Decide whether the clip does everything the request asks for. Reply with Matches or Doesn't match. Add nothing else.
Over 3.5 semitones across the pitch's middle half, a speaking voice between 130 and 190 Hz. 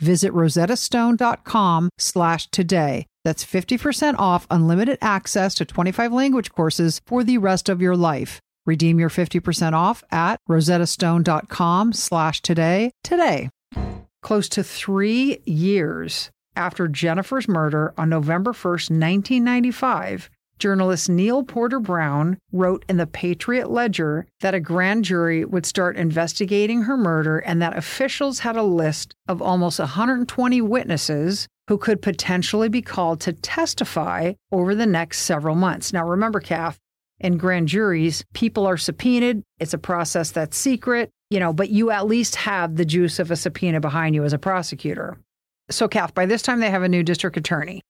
Matches